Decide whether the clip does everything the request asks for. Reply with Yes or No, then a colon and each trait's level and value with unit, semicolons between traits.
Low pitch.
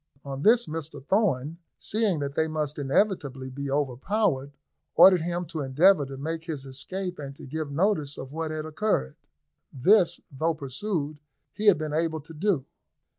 No: medium, 155 Hz